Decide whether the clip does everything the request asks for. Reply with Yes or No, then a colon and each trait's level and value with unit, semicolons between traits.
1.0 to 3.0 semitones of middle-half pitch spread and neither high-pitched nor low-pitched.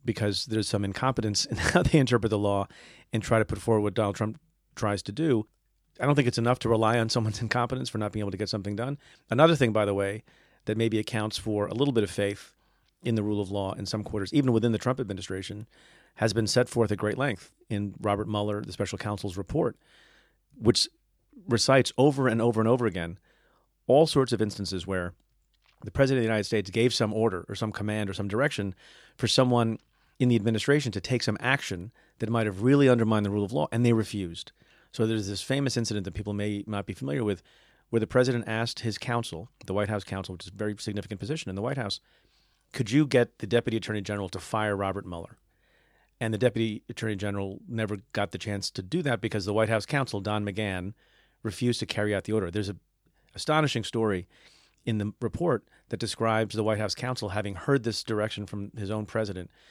No: narrow, 2.6 semitones; low, 110 Hz